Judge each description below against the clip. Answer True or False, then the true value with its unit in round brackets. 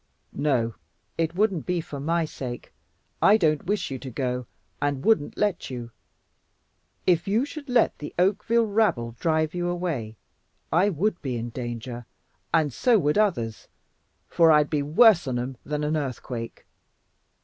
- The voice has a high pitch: False (155 Hz)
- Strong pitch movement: True (6.6 semitones)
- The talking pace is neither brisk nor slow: True (155 wpm)